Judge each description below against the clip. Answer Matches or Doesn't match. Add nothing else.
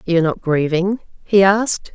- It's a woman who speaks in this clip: Matches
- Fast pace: Doesn't match